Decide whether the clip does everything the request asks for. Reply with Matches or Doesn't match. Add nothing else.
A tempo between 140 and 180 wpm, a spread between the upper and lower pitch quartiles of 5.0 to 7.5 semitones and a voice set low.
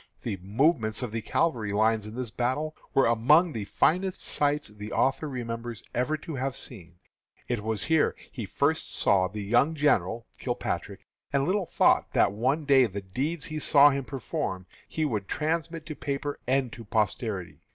Matches